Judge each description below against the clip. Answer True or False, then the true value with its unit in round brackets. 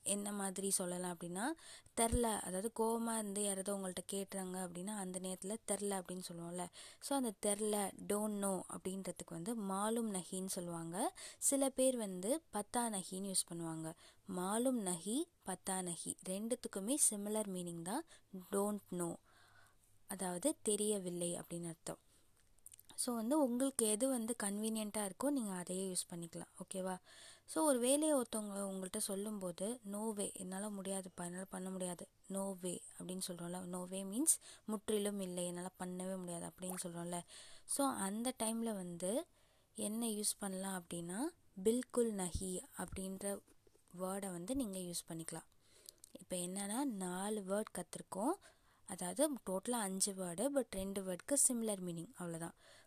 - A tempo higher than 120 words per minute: True (130 wpm)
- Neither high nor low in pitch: False (195 Hz)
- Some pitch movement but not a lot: True (3.5 semitones)